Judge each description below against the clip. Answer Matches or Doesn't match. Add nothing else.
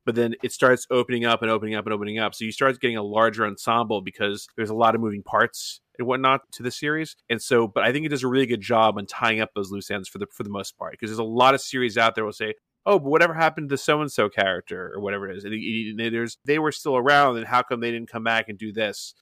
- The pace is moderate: Doesn't match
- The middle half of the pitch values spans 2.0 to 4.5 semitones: Matches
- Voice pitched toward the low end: Matches